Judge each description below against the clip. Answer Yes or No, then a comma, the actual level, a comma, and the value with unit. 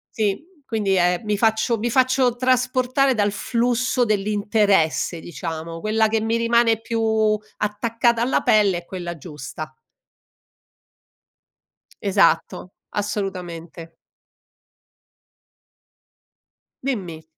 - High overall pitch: Yes, high, 210 Hz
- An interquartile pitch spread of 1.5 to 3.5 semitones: No, average, 4.6 semitones